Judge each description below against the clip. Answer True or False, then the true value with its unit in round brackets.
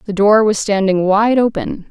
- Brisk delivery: False (190 wpm)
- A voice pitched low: False (205 Hz)